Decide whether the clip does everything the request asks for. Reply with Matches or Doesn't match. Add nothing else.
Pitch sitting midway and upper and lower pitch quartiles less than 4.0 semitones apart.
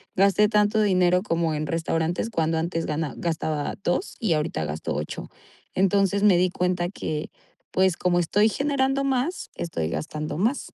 Doesn't match